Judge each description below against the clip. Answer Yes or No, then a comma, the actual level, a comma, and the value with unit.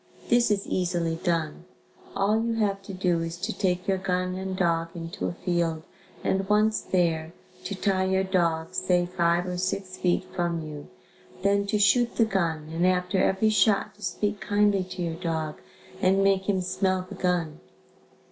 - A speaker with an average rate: Yes, average, 175 wpm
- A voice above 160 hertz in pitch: Yes, medium, 185 Hz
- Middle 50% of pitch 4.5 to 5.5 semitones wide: No, narrow, 2.5 semitones